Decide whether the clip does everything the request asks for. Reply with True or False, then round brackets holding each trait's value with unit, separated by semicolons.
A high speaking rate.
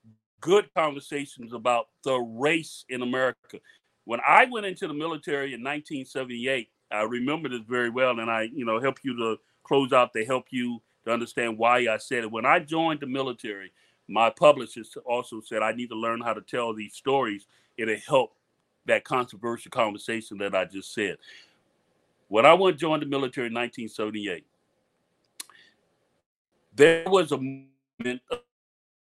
False (160 wpm)